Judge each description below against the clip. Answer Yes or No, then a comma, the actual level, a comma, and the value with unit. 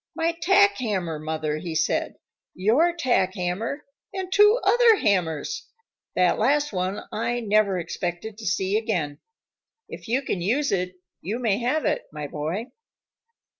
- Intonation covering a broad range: Yes, wide, 8.3 semitones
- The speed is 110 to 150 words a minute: Yes, average, 145 wpm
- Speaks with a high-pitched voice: Yes, high, 215 Hz